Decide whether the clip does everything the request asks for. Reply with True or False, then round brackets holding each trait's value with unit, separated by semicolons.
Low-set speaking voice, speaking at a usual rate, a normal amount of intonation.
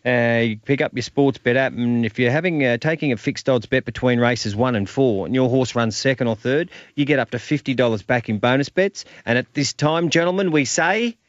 False (130 Hz; 250 wpm; 3.2 semitones)